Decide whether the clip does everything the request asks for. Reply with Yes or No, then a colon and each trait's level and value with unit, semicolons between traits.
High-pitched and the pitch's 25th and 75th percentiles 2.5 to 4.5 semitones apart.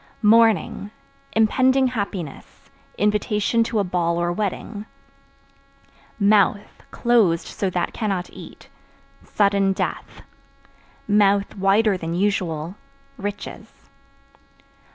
Yes: high, 200 Hz; average, 2.9 semitones